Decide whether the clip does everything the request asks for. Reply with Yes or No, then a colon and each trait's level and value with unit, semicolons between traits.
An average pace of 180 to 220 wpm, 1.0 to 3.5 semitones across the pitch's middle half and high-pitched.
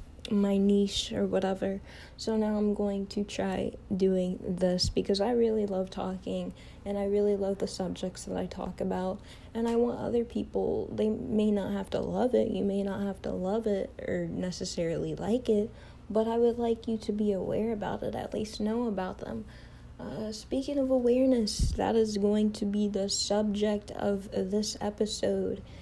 Yes: average, 185 wpm; narrow, 2.6 semitones; high, 205 Hz